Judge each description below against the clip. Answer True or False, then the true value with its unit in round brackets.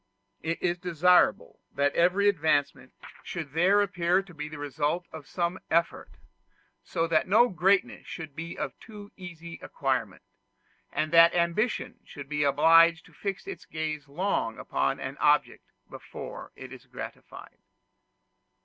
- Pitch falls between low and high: True (170 Hz)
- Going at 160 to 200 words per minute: False (140 wpm)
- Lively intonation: False (3.1 semitones)